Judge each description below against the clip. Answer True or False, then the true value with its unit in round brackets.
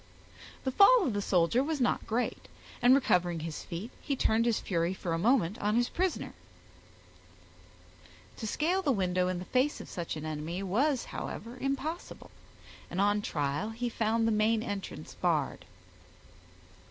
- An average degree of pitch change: False (6.2 semitones)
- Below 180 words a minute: True (160 wpm)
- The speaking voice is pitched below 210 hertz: False (215 Hz)